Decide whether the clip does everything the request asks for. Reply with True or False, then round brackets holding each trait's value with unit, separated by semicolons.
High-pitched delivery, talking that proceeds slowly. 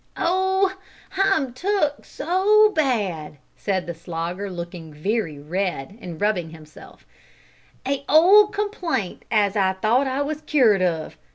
True (215 Hz; 125 wpm)